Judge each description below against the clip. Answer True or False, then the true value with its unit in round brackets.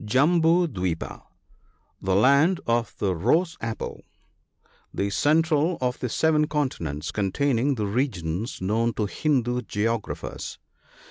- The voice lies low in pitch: True (120 Hz)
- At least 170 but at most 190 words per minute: False (140 wpm)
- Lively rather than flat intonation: True (6.7 semitones)